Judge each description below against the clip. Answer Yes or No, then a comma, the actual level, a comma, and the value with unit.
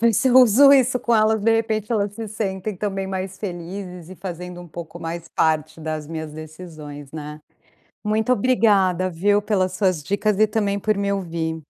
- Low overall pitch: No, high, 190 Hz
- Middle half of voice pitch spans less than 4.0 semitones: No, average, 4.3 semitones